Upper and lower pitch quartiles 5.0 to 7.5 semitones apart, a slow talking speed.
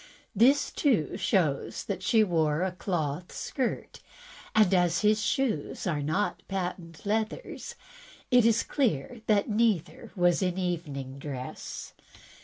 Yes: average, 5.3 semitones; slow, 125 wpm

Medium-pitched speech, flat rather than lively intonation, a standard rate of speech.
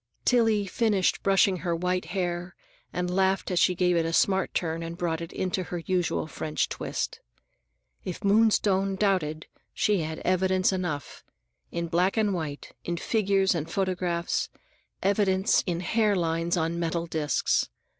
Yes: medium, 180 Hz; narrow, 2.3 semitones; average, 150 wpm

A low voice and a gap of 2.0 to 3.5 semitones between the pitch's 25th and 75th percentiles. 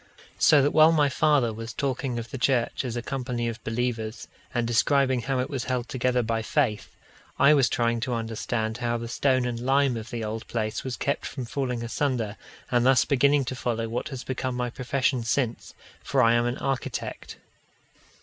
Yes: low, 125 Hz; narrow, 2.4 semitones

